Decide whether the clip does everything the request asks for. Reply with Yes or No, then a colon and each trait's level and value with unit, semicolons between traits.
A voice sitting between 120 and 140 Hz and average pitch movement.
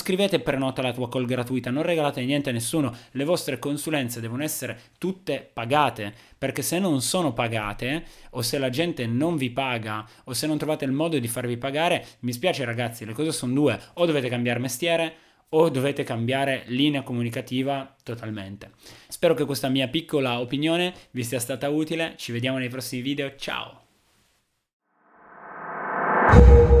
Yes: low, 135 Hz; average, 4.0 semitones